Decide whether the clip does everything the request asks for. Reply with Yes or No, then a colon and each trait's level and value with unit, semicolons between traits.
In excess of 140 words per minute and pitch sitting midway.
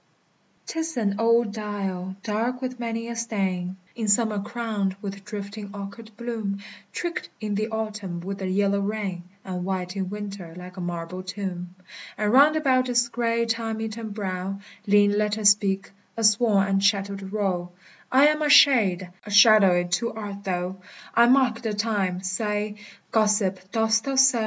No: average, 165 wpm; high, 205 Hz